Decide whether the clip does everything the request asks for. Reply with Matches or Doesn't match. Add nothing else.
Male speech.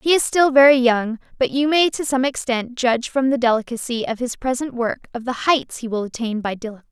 Doesn't match